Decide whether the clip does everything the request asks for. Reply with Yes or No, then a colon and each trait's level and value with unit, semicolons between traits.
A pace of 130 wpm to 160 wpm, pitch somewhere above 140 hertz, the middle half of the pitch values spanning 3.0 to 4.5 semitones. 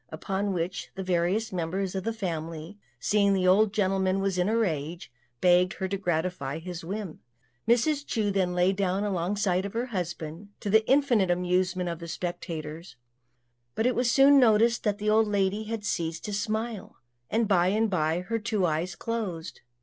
No: average, 180 wpm; high, 190 Hz; average, 3.4 semitones